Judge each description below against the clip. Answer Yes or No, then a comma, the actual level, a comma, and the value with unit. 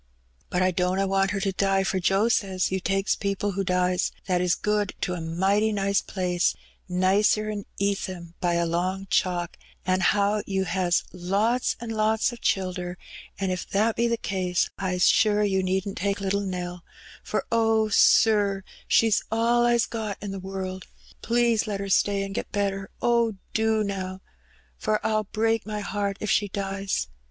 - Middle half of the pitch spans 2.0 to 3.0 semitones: Yes, narrow, 2.4 semitones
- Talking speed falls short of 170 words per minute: No, average, 175 wpm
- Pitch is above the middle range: Yes, high, 195 Hz